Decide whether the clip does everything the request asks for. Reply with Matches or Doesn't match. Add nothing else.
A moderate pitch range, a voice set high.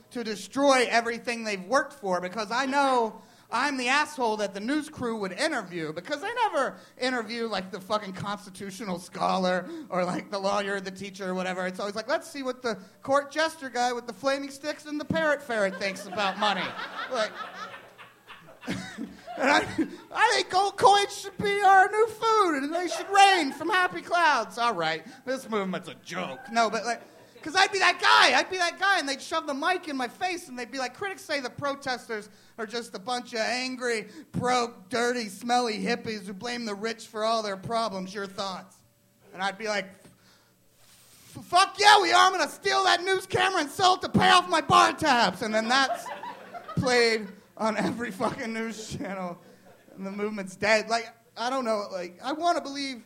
Doesn't match